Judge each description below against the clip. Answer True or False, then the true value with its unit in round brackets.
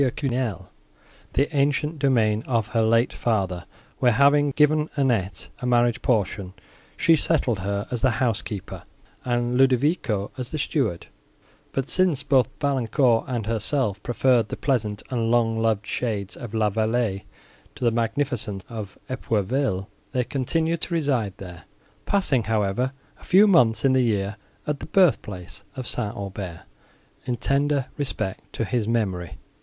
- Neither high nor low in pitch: False (120 Hz)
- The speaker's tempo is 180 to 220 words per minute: False (150 wpm)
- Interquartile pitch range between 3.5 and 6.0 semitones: True (4.4 semitones)